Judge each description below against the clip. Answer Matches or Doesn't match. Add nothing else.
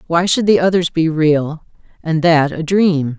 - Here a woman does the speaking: Matches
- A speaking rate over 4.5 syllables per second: Doesn't match